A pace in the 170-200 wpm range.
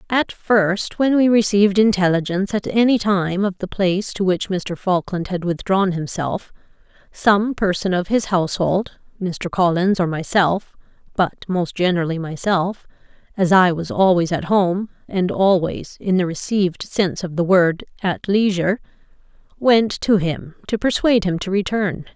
No: average, 155 wpm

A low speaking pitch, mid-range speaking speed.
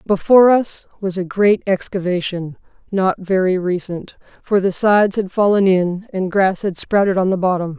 No: high, 190 Hz; average, 170 wpm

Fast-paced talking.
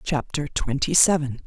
No: slow, 125 wpm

